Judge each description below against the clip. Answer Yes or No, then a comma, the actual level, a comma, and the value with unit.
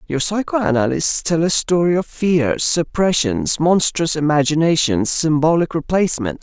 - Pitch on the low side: No, medium, 160 Hz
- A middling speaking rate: No, slow, 110 wpm